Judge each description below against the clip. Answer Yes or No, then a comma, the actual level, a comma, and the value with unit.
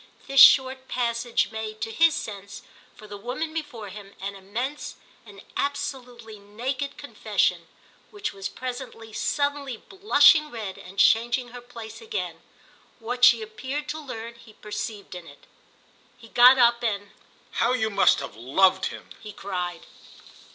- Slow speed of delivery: No, average, 145 wpm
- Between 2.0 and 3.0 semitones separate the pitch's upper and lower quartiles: No, average, 4.2 semitones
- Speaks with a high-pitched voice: Yes, high, 235 Hz